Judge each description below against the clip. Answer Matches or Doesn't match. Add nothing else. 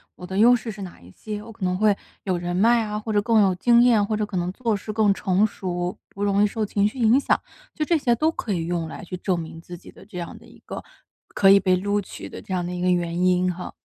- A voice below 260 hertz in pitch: Matches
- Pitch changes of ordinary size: Matches